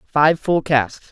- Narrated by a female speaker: No, male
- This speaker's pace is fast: No, average, 160 wpm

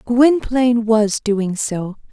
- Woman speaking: Yes, female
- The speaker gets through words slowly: Yes, slow, 115 wpm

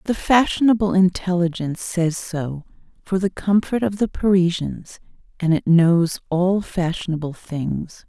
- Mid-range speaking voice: Yes, medium, 180 Hz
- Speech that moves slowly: Yes, slow, 125 wpm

